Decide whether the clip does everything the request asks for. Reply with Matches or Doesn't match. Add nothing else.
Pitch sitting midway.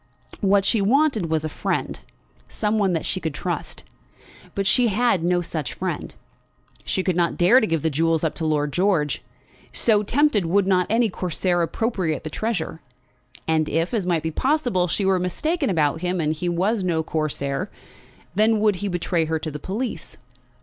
Matches